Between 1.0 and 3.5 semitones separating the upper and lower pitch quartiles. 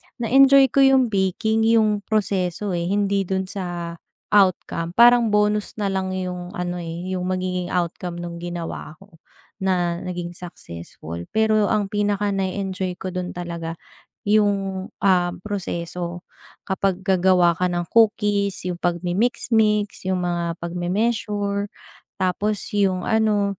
Yes: average, 2.8 semitones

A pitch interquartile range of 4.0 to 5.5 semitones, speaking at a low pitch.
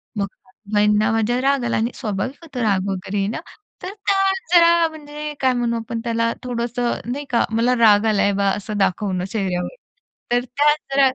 No: average, 4.5 semitones; high, 230 Hz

